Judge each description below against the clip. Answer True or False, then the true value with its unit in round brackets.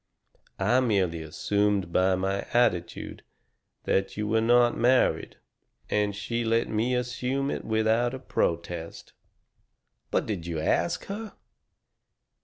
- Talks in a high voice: False (105 Hz)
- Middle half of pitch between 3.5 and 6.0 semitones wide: True (4.5 semitones)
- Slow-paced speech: True (120 wpm)